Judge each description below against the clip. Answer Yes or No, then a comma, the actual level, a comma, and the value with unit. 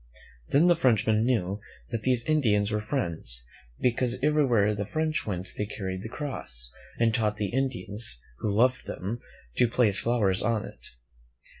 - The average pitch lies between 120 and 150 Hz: No, low, 110 Hz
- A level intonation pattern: No, average, 3.9 semitones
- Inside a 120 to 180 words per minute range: Yes, average, 160 wpm